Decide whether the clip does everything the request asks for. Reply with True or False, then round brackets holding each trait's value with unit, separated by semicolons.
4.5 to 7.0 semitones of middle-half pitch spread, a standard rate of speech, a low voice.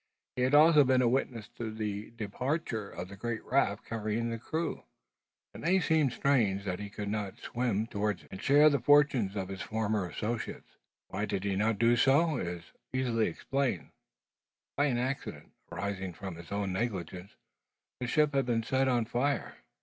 True (4.8 semitones; 180 wpm; 115 Hz)